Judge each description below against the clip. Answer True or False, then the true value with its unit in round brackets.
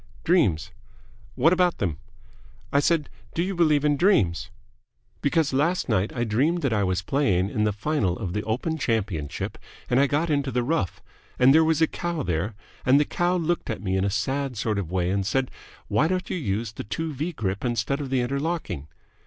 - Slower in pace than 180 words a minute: False (200 wpm)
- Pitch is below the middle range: True (130 Hz)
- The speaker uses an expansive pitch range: True (7.8 semitones)